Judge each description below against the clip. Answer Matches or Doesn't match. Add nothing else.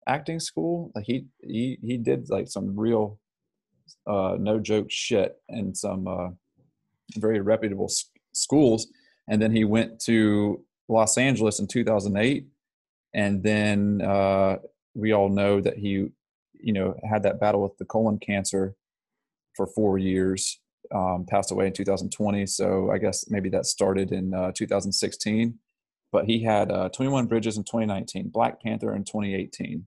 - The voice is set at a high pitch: Doesn't match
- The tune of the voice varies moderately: Doesn't match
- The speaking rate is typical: Matches